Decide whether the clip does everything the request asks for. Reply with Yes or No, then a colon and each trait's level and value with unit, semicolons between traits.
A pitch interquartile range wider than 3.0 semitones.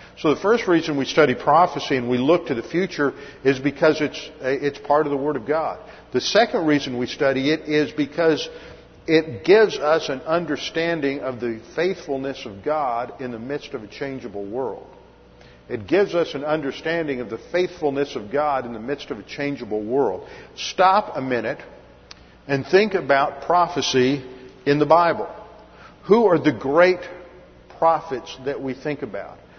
Yes: average, 3.6 semitones